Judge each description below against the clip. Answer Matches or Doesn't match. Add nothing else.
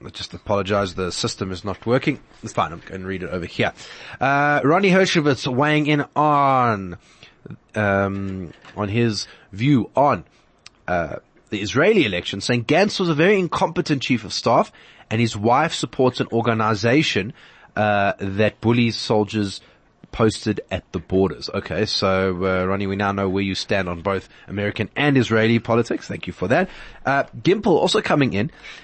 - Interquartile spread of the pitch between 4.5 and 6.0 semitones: Matches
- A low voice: Matches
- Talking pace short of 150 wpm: Doesn't match